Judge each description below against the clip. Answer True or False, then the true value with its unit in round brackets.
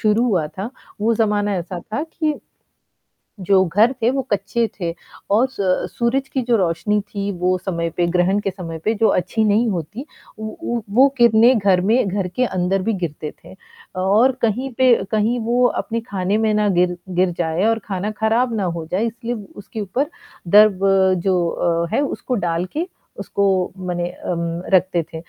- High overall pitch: True (205 Hz)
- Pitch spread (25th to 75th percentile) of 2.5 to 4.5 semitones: True (4.2 semitones)